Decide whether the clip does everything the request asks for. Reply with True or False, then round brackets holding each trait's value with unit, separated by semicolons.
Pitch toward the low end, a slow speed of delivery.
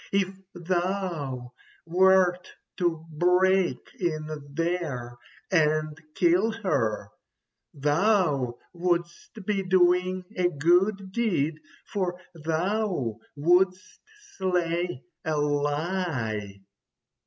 False (175 Hz; 80 wpm)